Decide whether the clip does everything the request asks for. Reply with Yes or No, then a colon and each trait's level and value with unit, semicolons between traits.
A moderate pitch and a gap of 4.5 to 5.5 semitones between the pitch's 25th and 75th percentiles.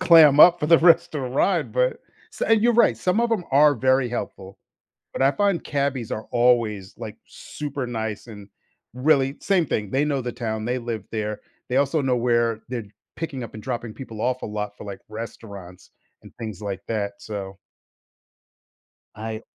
No: low, 120 Hz; average, 4.9 semitones